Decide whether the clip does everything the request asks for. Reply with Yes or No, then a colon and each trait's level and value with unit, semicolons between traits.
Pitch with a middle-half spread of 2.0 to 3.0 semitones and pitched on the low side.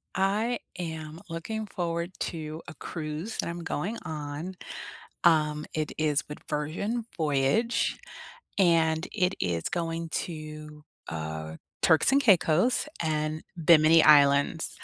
No: average, 2.7 semitones; medium, 160 Hz